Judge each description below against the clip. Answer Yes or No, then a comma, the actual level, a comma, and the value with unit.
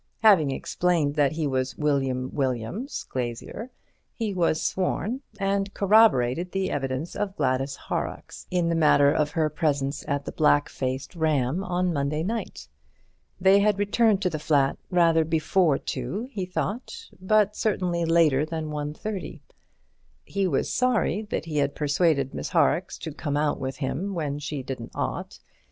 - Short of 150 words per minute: No, average, 155 wpm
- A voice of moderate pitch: Yes, medium, 160 Hz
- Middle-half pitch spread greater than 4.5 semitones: Yes, average, 5.3 semitones